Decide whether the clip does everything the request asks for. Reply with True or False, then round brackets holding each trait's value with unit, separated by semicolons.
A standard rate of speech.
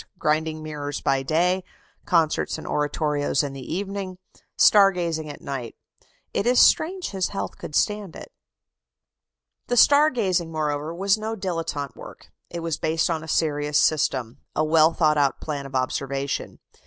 True (155 wpm)